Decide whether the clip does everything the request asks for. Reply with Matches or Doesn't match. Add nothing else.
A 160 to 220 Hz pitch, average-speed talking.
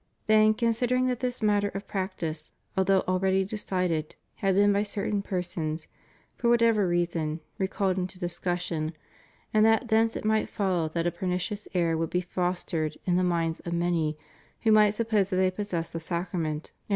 Matches